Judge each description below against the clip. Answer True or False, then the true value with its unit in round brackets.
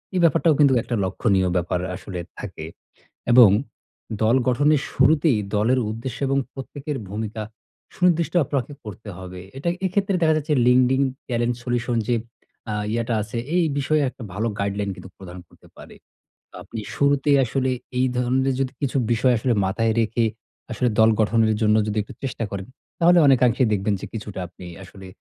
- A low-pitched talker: True (120 Hz)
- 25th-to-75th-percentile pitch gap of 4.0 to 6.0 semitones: True (4.4 semitones)